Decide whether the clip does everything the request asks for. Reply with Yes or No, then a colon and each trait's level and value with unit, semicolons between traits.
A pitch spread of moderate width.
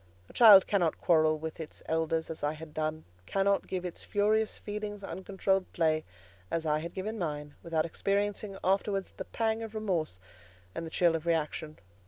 Yes: average, 4.1 semitones